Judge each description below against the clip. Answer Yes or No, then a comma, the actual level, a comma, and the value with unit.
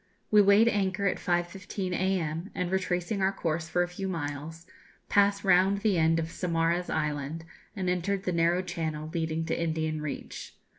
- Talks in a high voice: No, medium, 175 Hz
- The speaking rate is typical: Yes, average, 165 wpm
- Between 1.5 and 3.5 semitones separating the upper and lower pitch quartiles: Yes, average, 2.8 semitones